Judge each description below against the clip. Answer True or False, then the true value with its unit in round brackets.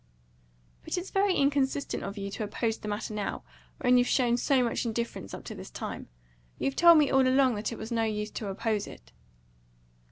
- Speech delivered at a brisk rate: True (210 wpm)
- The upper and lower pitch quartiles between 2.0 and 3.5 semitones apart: False (4.1 semitones)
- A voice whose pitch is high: True (235 Hz)